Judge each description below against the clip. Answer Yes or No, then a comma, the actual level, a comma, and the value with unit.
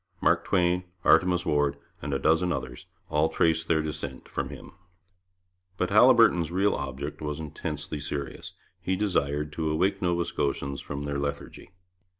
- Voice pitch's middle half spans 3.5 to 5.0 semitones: Yes, average, 3.8 semitones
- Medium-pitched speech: No, very low, 80 Hz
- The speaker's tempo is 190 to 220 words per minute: No, average, 150 wpm